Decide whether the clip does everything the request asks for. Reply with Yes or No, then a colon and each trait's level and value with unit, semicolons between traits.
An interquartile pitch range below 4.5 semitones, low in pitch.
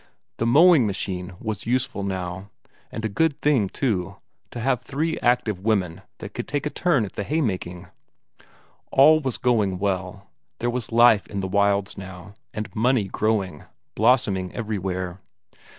No: average, 4.8 semitones; low, 105 Hz